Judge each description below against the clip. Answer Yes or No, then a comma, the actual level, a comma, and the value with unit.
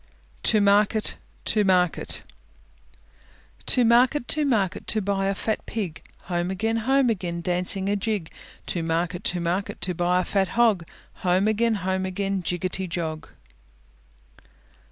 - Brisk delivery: No, average, 140 wpm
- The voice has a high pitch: Yes, high, 195 Hz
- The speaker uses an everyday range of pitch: Yes, average, 3.4 semitones